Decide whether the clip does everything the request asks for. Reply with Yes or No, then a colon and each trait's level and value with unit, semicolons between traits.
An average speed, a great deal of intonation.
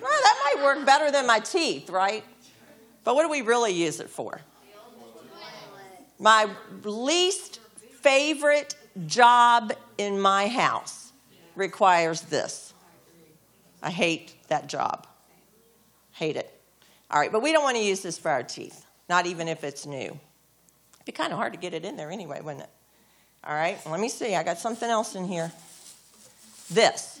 Yes: average, 165 wpm; wide, 7.3 semitones